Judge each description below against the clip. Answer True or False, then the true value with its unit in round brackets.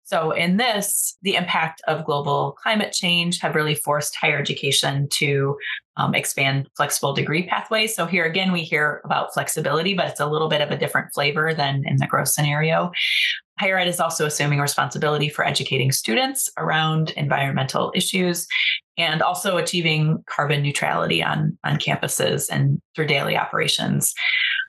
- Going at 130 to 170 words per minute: True (160 wpm)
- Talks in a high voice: False (155 Hz)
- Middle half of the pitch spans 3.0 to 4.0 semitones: True (3.5 semitones)